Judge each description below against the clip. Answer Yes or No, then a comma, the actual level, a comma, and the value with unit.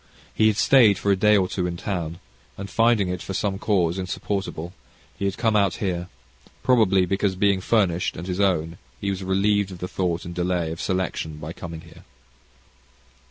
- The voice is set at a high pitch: No, very low, 95 Hz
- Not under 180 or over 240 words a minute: Yes, average, 185 wpm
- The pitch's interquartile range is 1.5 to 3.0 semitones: Yes, narrow, 2.5 semitones